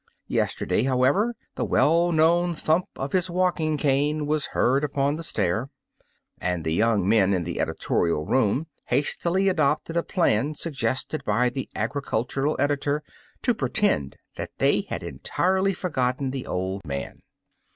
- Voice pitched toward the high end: No, medium, 140 Hz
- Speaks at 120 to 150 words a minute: Yes, average, 140 wpm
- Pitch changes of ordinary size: No, wide, 6.5 semitones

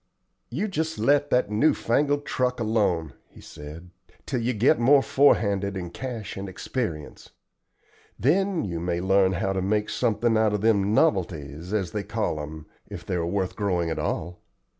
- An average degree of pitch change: No, wide, 5.9 semitones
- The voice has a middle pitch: No, low, 105 Hz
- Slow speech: No, average, 170 wpm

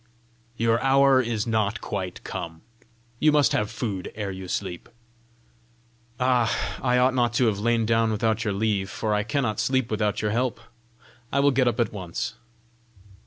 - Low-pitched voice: Yes, low, 110 Hz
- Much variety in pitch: No, average, 3.2 semitones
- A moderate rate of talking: Yes, average, 165 wpm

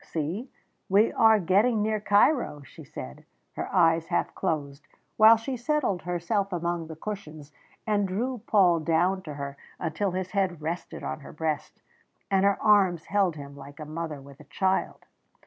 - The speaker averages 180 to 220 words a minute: No, average, 165 wpm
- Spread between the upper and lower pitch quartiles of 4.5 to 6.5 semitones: Yes, average, 4.8 semitones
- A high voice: No, medium, 180 Hz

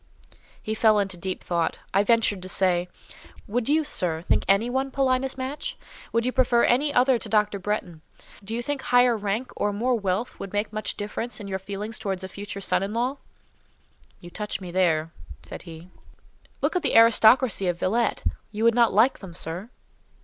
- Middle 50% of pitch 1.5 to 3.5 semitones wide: No, average, 4.2 semitones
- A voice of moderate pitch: No, high, 210 Hz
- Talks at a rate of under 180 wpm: No, average, 185 wpm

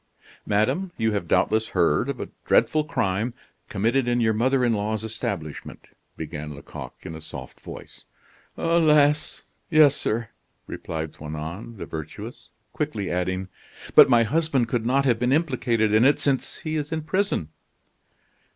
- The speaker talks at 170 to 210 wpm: No, average, 150 wpm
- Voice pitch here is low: Yes, low, 115 Hz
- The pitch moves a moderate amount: No, wide, 6.6 semitones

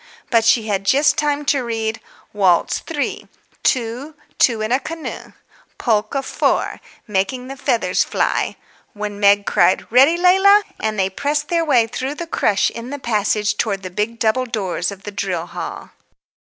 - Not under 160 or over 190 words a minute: Yes, average, 165 wpm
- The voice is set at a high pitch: Yes, high, 230 Hz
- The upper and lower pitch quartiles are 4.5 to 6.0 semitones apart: Yes, wide, 5.4 semitones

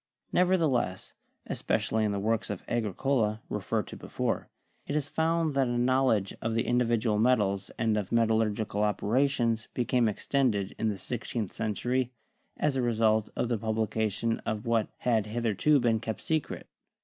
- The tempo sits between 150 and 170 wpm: Yes, average, 155 wpm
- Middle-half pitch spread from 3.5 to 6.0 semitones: No, average, 2.8 semitones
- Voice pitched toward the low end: Yes, low, 115 Hz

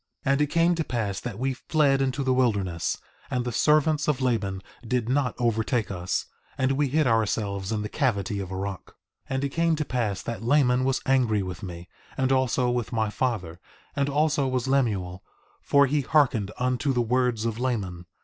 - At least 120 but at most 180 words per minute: No, average, 195 wpm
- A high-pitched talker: No, low, 125 Hz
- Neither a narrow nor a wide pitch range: Yes, average, 4.5 semitones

